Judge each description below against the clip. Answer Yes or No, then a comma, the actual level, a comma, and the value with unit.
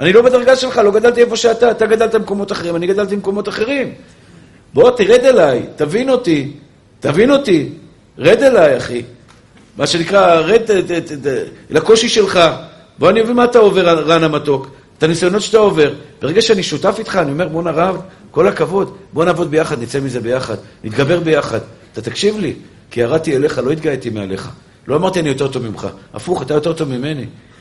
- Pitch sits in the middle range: Yes, medium, 165 Hz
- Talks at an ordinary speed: No, fast, 180 wpm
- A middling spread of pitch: No, wide, 7.6 semitones